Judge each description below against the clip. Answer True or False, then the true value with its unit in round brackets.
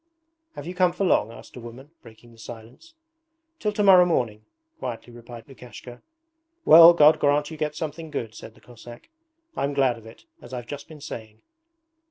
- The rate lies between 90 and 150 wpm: False (185 wpm)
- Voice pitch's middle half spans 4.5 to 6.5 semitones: True (5.4 semitones)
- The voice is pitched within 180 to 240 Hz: False (130 Hz)